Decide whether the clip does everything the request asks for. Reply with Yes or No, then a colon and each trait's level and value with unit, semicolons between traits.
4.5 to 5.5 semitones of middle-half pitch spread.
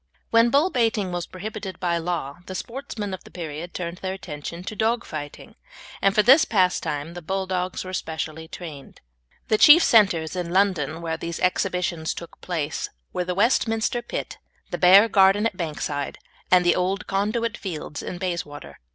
No: average, 3.7 semitones